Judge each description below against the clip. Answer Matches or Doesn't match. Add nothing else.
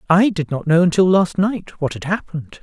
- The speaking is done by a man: Matches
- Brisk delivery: Matches